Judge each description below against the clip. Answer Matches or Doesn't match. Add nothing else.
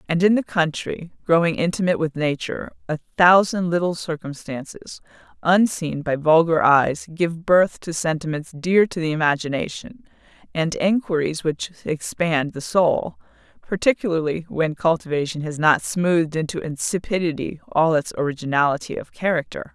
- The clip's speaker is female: Matches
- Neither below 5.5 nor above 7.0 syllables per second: Doesn't match